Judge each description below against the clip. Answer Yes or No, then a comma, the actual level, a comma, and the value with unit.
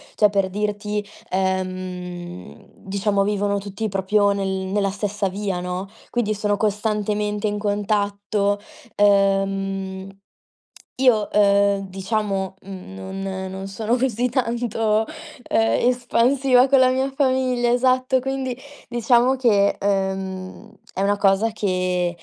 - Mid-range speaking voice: No, high, 205 Hz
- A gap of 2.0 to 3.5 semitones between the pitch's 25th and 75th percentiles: Yes, narrow, 2.6 semitones